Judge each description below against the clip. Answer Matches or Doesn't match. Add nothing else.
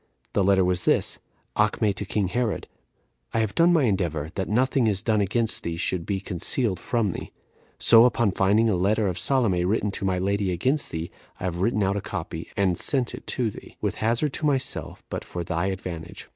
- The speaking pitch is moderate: Doesn't match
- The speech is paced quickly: Matches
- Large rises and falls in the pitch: Doesn't match